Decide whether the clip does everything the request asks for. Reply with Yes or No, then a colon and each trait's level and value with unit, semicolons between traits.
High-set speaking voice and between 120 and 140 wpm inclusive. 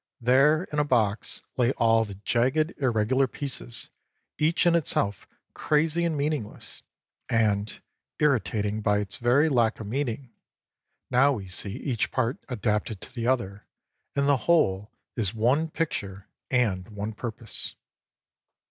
No: low, 120 Hz; slow, 135 wpm